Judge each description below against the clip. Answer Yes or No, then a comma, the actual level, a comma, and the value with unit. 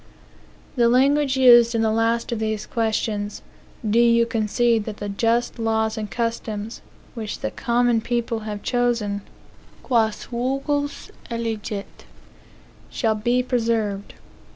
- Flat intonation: Yes, narrow, 1.7 semitones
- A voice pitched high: Yes, high, 230 Hz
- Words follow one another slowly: Yes, slow, 125 wpm